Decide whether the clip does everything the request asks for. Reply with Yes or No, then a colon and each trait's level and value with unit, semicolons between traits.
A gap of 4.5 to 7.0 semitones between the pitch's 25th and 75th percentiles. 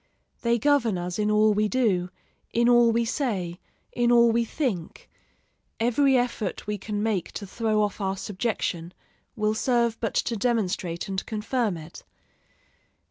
No: average, 3.4 semitones